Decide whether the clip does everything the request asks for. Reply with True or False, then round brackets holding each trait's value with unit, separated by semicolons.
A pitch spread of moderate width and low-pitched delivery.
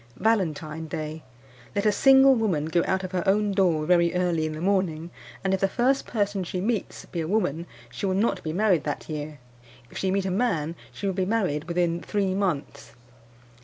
False (4.0 semitones; 185 Hz)